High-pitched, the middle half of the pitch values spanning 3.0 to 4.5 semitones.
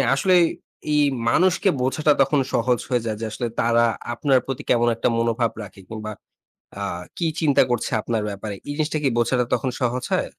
No: low, 125 Hz; average, 3.7 semitones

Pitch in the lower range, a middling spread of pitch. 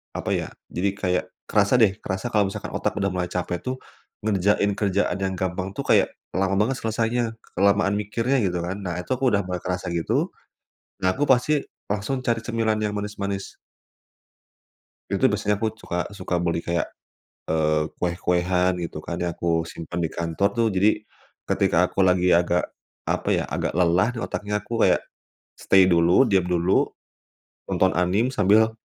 Yes: very low, 95 Hz; average, 3.2 semitones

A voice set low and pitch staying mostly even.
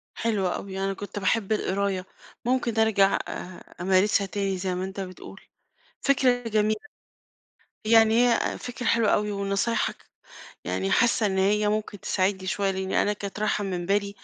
No: high, 200 Hz; narrow, 2.3 semitones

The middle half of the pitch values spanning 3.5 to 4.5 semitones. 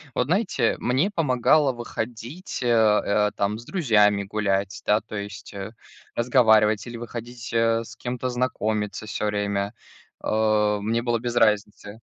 No: average, 2.7 semitones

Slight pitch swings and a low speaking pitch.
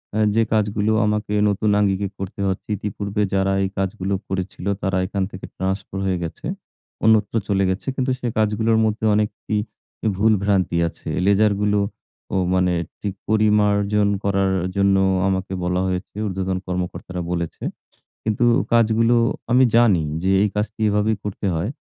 Yes: narrow, 1.9 semitones; low, 100 Hz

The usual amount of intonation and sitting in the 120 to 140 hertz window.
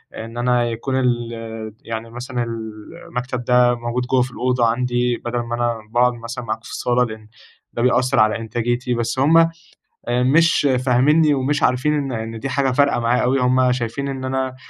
No: narrow, 1.8 semitones; low, 125 Hz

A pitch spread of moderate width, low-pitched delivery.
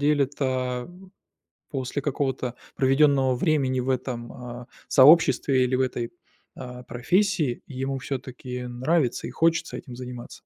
No: narrow, 2.3 semitones; low, 130 Hz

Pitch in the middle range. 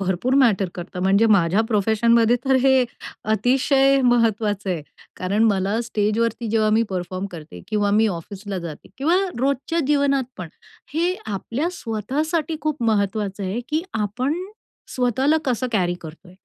No: high, 220 Hz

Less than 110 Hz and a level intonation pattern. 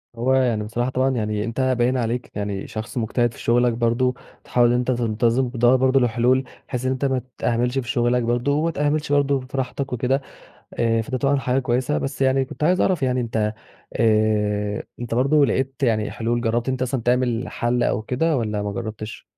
No: low, 125 Hz; narrow, 2.3 semitones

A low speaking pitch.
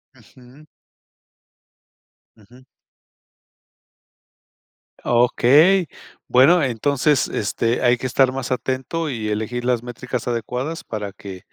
Yes: low, 125 Hz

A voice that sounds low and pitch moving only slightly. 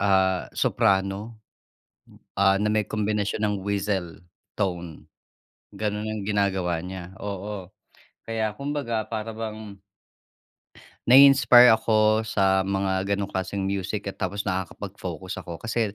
Yes: low, 100 Hz; narrow, 2.2 semitones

